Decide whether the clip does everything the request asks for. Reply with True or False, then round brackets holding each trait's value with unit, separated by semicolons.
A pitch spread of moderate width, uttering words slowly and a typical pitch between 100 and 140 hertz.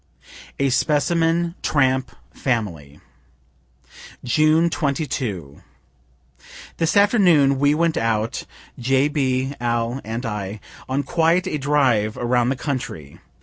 True (4.9 semitones; 105 wpm; 135 Hz)